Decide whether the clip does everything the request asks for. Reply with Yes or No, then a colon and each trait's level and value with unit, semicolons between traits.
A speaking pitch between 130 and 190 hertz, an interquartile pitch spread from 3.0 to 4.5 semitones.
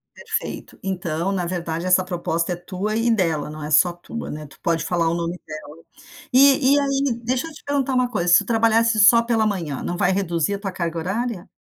No: medium, 185 Hz; wide, 5.4 semitones